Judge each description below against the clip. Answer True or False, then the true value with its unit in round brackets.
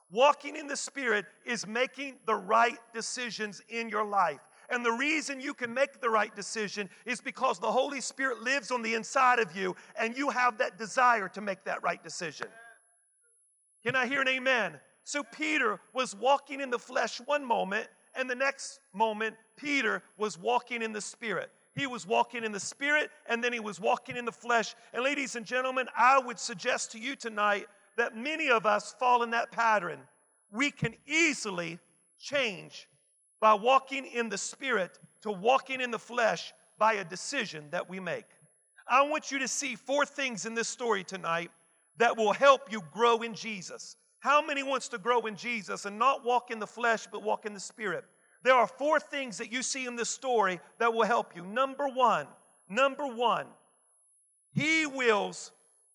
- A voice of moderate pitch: False (235 Hz)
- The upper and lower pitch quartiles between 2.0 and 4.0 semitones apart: True (3.6 semitones)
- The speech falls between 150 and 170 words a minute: False (185 wpm)